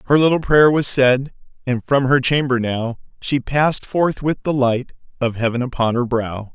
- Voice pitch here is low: Yes, low, 130 Hz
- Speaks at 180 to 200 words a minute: Yes, average, 190 wpm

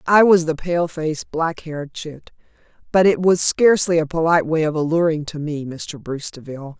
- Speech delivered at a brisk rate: No, average, 195 wpm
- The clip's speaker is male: No, female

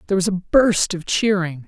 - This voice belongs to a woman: Yes, female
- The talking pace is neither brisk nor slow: No, fast, 215 wpm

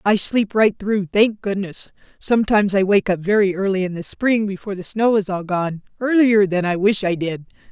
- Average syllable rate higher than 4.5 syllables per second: Yes, 5.2 syllables/s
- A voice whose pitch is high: Yes, high, 200 Hz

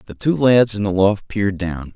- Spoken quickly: Yes, fast, 245 wpm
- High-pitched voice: No, low, 105 Hz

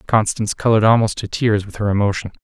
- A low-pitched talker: Yes, low, 105 Hz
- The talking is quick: No, average, 195 wpm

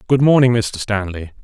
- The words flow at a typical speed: Yes, average, 170 wpm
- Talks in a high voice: No, low, 110 Hz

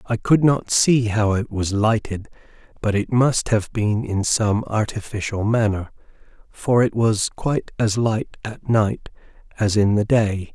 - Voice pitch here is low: Yes, low, 110 Hz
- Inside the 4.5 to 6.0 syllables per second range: No, 4.0 syllables/s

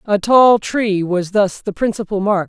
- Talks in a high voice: Yes, high, 205 Hz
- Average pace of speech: Yes, average, 195 wpm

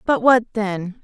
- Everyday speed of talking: Yes, average, 175 wpm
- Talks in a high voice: Yes, high, 215 Hz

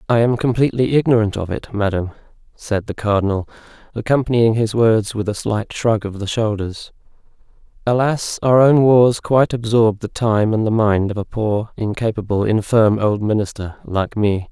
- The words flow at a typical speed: Yes, average, 165 wpm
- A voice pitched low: Yes, low, 110 Hz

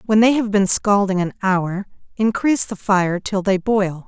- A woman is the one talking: Yes, female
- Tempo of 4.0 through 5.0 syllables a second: Yes, 4.5 syllables/s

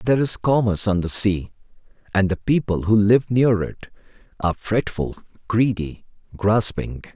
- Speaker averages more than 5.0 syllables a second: No, 4.7 syllables/s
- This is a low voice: Yes, low, 105 Hz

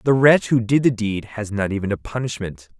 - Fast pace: Yes, fast, 235 wpm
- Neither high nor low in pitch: No, low, 115 Hz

